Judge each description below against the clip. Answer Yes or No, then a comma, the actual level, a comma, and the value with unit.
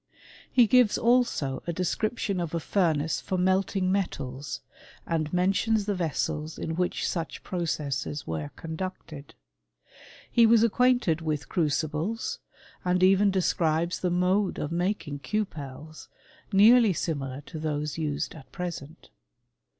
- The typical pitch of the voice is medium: Yes, medium, 175 Hz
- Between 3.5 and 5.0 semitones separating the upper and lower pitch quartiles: Yes, average, 4.4 semitones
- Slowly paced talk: Yes, slow, 130 wpm